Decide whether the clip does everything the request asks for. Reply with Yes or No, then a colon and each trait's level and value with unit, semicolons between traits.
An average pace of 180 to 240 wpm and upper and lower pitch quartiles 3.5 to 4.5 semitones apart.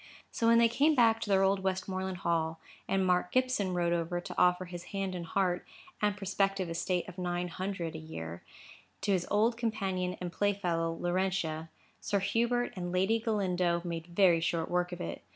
No: average, 190 wpm; narrow, 2.4 semitones